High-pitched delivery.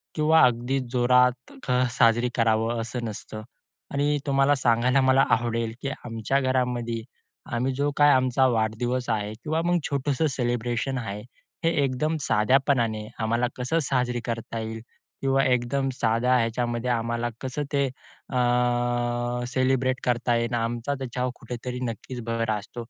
No: low, 125 Hz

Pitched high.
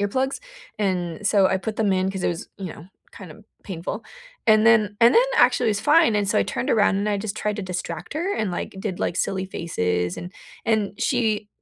Yes: high, 205 Hz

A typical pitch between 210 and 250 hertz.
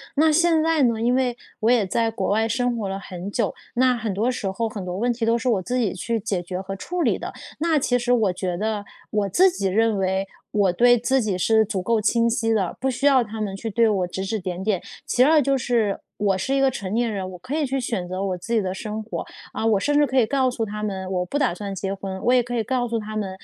Yes: high, 220 Hz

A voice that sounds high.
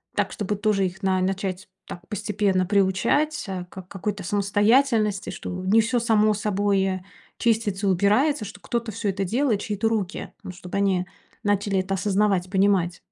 Yes: high, 200 Hz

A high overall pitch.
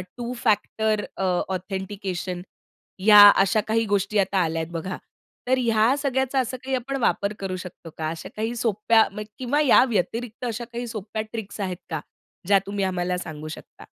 Yes: high, 210 Hz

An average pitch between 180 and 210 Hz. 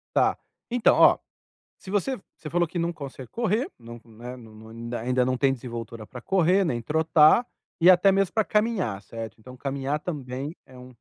No: medium, 140 Hz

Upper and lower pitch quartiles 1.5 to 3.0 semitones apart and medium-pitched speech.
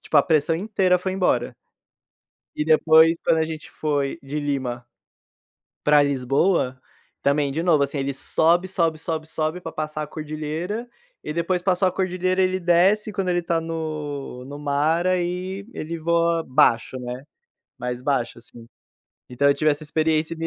No: average, 3.6 semitones; medium, 155 Hz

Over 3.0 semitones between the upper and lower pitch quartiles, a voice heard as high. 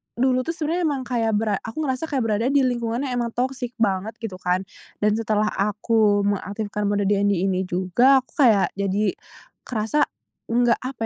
Yes: average, 3.8 semitones; high, 225 Hz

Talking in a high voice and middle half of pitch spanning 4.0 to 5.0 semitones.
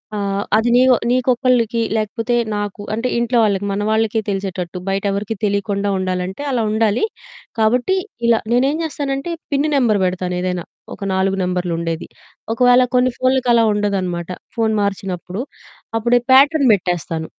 Yes: high, 215 Hz; average, 4.6 semitones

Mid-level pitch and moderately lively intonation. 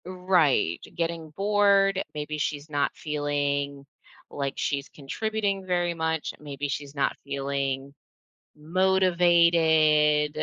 Yes: medium, 155 Hz; average, 4.0 semitones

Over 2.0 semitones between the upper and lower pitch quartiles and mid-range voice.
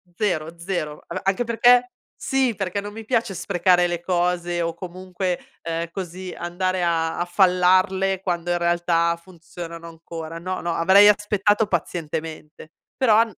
Yes: narrow, 2.4 semitones; medium, 180 Hz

